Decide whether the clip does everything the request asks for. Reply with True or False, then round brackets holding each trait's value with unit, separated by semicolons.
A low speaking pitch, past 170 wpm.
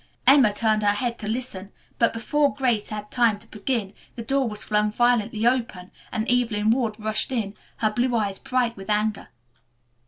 False (220 Hz; 180 wpm)